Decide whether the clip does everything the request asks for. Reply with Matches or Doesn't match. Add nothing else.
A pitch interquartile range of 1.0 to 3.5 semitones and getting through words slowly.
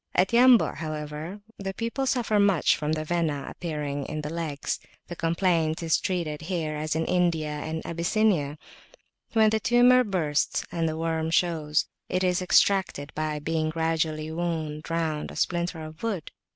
Doesn't match